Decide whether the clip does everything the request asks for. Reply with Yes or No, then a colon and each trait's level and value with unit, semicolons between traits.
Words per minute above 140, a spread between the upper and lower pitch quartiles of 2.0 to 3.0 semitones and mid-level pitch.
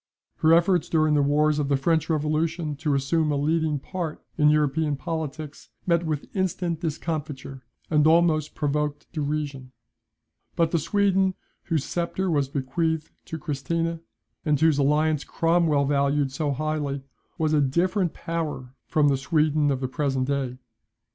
Yes: average, 150 wpm; narrow, 2.5 semitones; medium, 155 Hz